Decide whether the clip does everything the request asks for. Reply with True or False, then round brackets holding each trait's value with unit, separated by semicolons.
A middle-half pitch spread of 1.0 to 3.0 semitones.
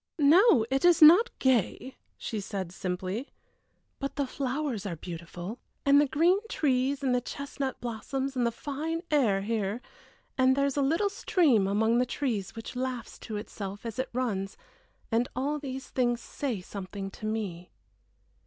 False (5.2 semitones)